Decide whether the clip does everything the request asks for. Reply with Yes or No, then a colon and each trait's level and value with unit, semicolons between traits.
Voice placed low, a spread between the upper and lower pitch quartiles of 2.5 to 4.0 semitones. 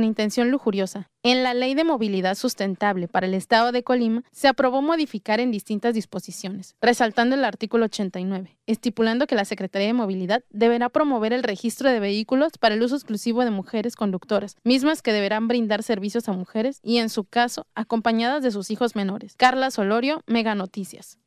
No: high, 225 Hz; average, 3.2 semitones